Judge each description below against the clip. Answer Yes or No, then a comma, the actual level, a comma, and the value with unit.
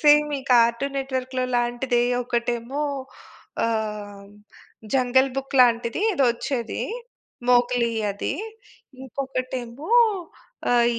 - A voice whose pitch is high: Yes, high, 245 Hz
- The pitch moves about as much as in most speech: No, narrow, 2.3 semitones